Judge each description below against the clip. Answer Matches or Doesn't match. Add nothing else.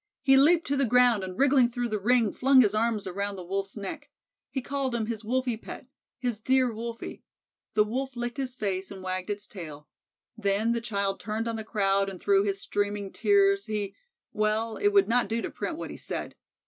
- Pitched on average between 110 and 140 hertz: Doesn't match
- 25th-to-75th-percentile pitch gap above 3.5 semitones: Matches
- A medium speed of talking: Doesn't match